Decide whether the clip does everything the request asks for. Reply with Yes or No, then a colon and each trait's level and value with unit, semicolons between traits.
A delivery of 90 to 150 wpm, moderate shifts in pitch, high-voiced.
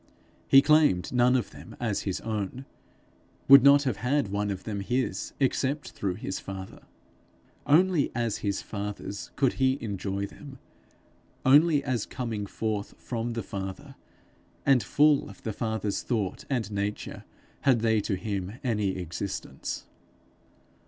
No: average, 140 wpm; average, 4.8 semitones; low, 110 Hz